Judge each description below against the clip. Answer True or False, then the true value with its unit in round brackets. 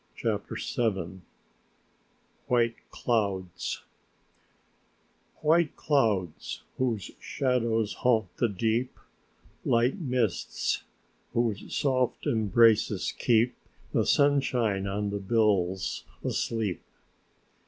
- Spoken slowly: True (80 wpm)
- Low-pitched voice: True (115 Hz)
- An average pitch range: True (3.7 semitones)